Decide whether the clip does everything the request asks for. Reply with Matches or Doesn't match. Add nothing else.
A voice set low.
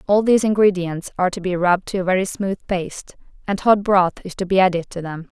Doesn't match